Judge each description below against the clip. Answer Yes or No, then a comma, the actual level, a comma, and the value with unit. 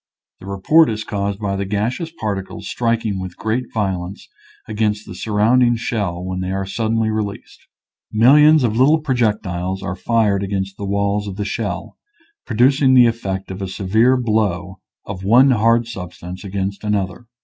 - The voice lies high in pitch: No, low, 105 Hz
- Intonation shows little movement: No, average, 3.3 semitones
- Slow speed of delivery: No, average, 165 wpm